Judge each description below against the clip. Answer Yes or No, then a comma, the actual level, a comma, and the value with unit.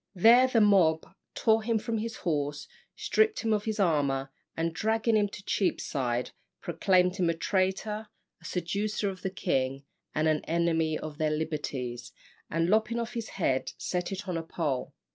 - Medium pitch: Yes, medium, 180 Hz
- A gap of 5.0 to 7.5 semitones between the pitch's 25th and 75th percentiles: Yes, wide, 5.6 semitones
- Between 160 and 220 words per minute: Yes, average, 170 wpm